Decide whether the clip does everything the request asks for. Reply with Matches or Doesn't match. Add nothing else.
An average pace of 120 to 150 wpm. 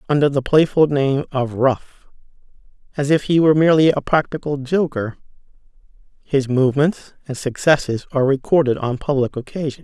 Matches